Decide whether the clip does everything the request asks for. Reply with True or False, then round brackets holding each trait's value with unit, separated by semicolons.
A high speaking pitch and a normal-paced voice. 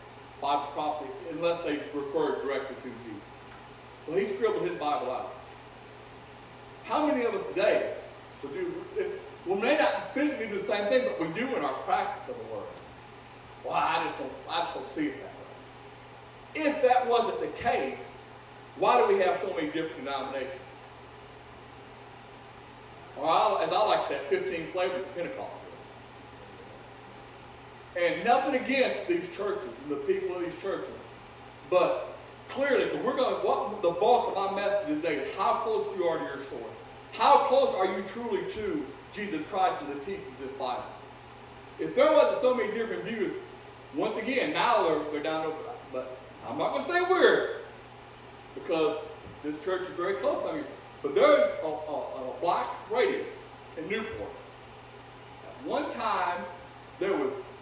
True (225 Hz; 165 wpm)